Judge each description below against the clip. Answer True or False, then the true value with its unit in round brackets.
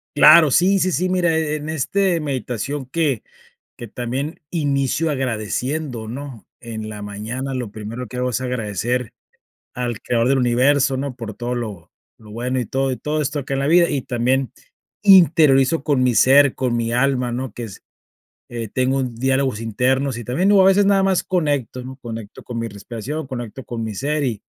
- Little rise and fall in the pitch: False (3.6 semitones)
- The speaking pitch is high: False (130 Hz)